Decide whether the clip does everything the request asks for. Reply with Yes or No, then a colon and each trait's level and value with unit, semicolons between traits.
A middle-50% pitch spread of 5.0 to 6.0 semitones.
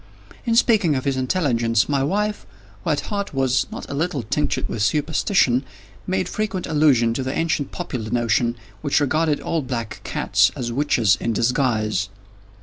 Yes: wide, 5.4 semitones